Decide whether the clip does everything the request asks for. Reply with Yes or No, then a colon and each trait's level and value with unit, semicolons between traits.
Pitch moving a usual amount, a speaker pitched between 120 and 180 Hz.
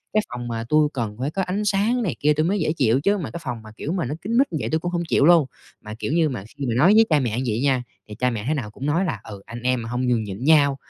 No: wide, 6.2 semitones; medium, 140 Hz